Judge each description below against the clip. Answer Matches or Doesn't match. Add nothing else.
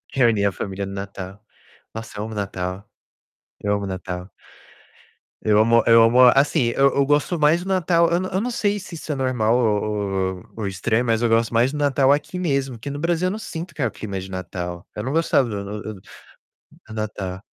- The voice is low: Matches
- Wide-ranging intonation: Matches